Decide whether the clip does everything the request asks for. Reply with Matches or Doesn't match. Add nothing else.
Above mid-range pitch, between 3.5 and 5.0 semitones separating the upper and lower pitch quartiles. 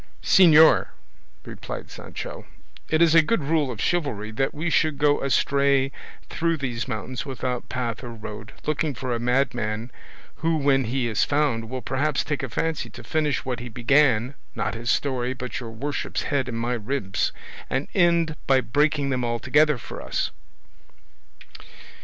Doesn't match